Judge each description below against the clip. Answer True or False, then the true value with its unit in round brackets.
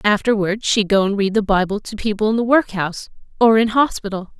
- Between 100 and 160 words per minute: False (205 wpm)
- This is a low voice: False (210 Hz)